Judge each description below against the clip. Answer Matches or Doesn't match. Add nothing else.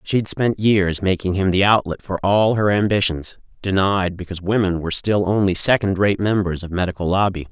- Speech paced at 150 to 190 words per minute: Matches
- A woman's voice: Doesn't match